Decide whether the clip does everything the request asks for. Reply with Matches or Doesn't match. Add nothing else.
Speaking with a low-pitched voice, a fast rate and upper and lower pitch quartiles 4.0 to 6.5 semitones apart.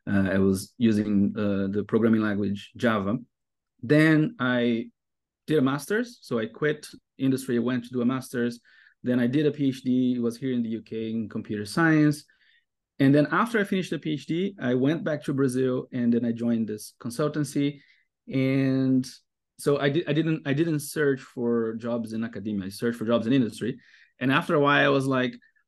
Doesn't match